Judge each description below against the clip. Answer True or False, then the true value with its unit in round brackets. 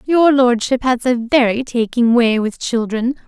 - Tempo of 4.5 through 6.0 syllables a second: False (4.2 syllables/s)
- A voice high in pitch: True (245 Hz)